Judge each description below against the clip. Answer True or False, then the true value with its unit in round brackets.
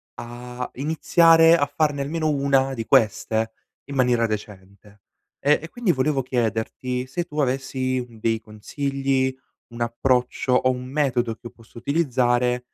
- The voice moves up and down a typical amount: True (3.1 semitones)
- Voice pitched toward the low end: True (130 Hz)